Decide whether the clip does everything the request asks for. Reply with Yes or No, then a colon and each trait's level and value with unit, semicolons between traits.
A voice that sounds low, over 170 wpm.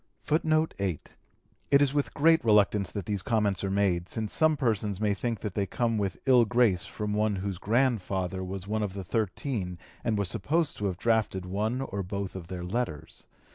Yes: low, 105 Hz; average, 195 wpm